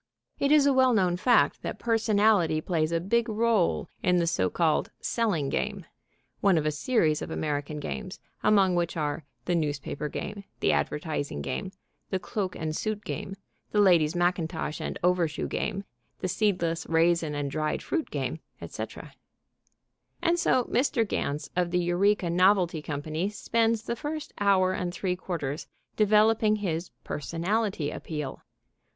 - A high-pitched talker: No, medium, 180 Hz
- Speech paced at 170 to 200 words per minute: No, average, 155 wpm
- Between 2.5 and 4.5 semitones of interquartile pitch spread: No, average, 5.2 semitones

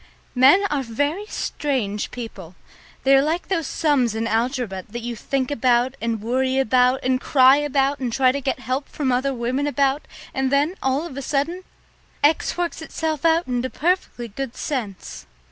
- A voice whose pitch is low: No, very high, 265 Hz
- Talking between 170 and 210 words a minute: Yes, average, 175 wpm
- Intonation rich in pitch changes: No, average, 3.1 semitones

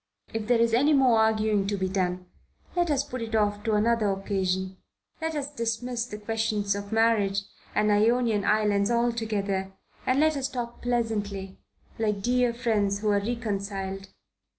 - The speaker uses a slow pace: No, average, 160 wpm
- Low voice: No, high, 220 Hz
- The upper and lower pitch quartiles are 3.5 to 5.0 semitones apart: No, average, 2.9 semitones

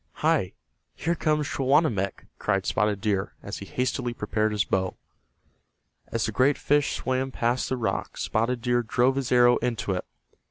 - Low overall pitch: Yes, low, 120 Hz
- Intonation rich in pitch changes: No, average, 3.6 semitones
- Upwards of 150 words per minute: Yes, average, 160 wpm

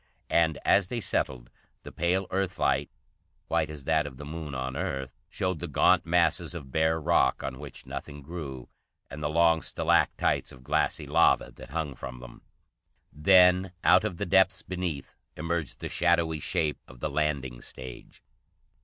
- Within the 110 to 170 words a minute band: Yes, average, 165 wpm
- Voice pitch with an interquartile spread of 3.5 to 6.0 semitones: Yes, average, 4.2 semitones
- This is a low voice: Yes, very low, 80 Hz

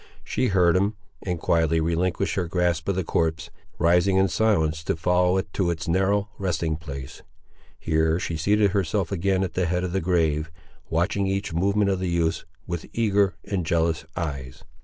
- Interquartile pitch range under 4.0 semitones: Yes, average, 3.0 semitones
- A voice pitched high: No, very low, 90 Hz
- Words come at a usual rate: Yes, average, 180 wpm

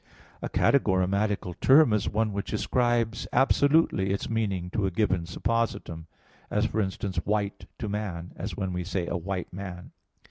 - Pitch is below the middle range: Yes, low, 100 Hz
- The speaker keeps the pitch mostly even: No, average, 3.3 semitones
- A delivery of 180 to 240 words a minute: No, average, 155 wpm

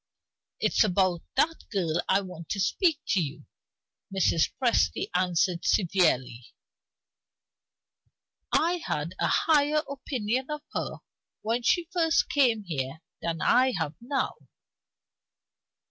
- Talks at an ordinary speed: No, slow, 115 wpm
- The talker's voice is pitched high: Yes, high, 200 Hz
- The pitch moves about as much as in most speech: No, wide, 8.8 semitones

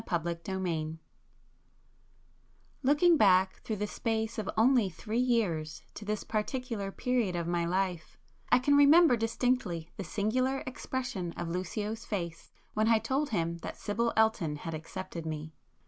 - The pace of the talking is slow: No, average, 145 wpm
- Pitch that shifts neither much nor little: No, wide, 5.8 semitones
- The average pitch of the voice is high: Yes, high, 210 Hz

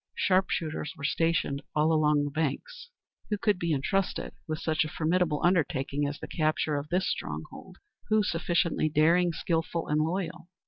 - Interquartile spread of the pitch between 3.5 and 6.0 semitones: No, average, 2.9 semitones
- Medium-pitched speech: Yes, medium, 160 Hz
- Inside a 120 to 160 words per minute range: Yes, average, 155 wpm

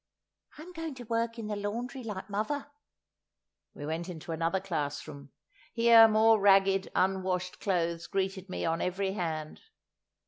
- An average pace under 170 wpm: Yes, average, 140 wpm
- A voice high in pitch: Yes, high, 195 Hz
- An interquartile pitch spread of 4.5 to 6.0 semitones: Yes, average, 4.8 semitones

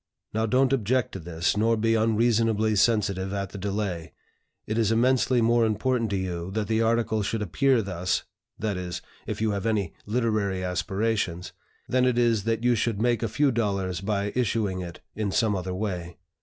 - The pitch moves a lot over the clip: No, average, 3.0 semitones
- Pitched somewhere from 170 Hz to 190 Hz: No, low, 110 Hz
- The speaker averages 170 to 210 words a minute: Yes, average, 185 wpm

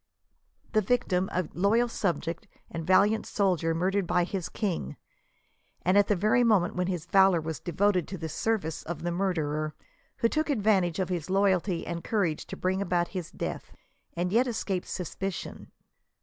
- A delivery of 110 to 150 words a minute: No, average, 175 wpm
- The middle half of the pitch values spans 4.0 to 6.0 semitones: No, average, 2.9 semitones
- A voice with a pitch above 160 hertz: Yes, medium, 185 Hz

